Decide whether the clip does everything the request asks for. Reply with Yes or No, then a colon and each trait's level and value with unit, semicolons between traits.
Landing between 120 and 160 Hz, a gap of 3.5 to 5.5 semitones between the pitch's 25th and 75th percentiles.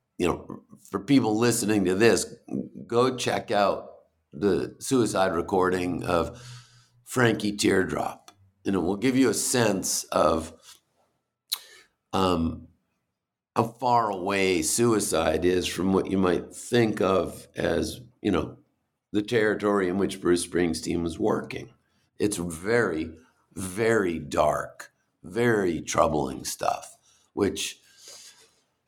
No: low, 100 Hz; average, 5.0 semitones